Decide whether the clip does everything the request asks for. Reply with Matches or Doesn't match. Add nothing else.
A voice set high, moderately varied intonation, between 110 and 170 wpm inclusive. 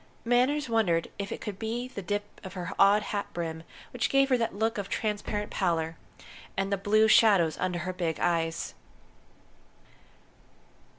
Matches